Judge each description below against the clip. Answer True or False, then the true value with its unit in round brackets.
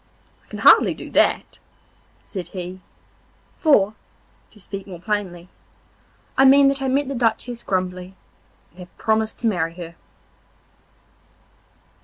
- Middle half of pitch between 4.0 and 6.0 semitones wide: True (5.0 semitones)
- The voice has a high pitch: True (200 Hz)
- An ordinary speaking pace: False (130 wpm)